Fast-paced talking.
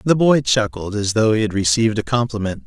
Yes: fast, 225 wpm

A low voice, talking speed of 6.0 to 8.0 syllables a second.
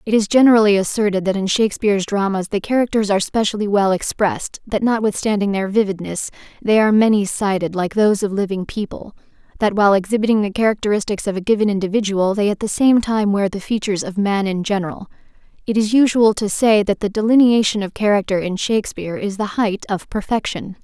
No: high, 205 Hz; 6.2 syllables/s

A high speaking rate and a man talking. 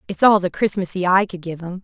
No: fast, 260 wpm; female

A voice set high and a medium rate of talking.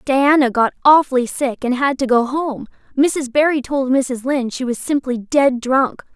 Yes: very high, 265 Hz; average, 185 wpm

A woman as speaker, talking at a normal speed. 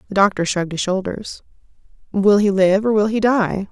Yes: female; average, 195 wpm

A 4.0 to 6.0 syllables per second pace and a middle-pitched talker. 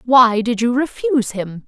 No: 4.5 syllables/s; high, 240 Hz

